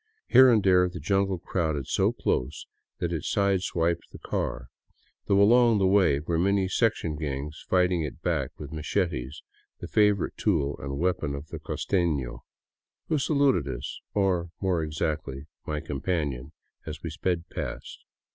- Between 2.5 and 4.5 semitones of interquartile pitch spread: No, average, 4.9 semitones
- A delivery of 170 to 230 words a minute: No, average, 160 wpm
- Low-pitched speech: Yes, very low, 85 Hz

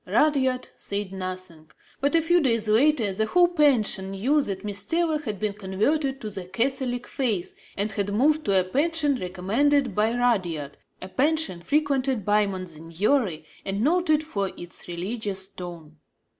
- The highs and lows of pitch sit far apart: Yes, wide, 7.0 semitones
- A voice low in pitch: No, high, 215 Hz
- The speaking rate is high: No, average, 155 wpm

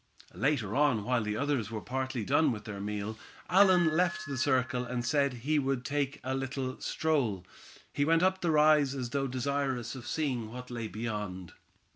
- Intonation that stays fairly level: No, average, 3.8 semitones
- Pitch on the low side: Yes, low, 130 Hz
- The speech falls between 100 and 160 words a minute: No, average, 180 wpm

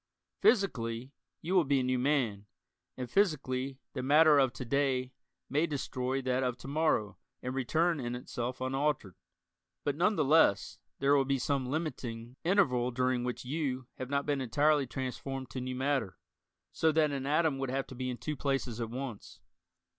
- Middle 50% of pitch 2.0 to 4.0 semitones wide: Yes, narrow, 2.5 semitones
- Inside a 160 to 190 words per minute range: Yes, average, 175 wpm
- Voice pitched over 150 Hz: No, low, 135 Hz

